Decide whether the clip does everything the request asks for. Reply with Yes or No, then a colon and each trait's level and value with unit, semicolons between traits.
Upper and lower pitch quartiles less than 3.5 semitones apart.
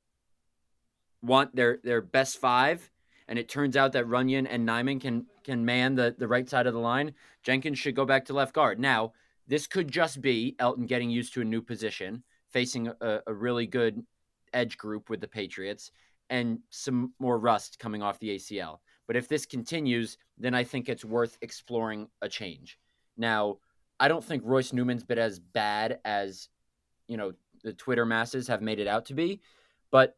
Yes: average, 2.9 semitones